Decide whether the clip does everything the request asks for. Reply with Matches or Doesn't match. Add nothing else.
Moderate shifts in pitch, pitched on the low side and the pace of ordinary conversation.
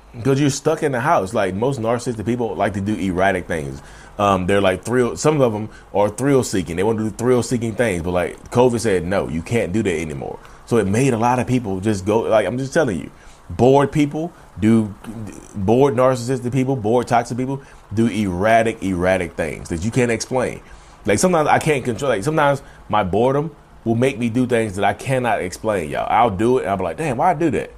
Doesn't match